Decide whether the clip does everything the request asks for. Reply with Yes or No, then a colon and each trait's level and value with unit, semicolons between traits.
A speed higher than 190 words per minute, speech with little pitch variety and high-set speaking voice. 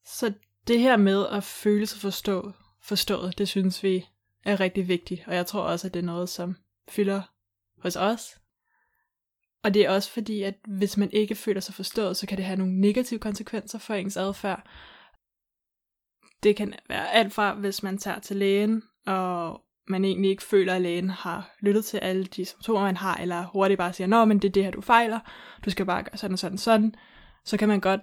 Yes: average, 210 wpm; narrow, 1.9 semitones; high, 195 Hz